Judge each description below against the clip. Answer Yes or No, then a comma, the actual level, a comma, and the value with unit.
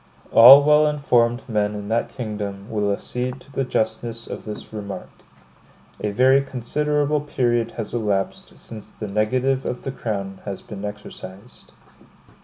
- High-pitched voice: No, low, 115 Hz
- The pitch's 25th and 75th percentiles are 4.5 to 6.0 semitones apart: No, average, 4.0 semitones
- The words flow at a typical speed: Yes, average, 145 wpm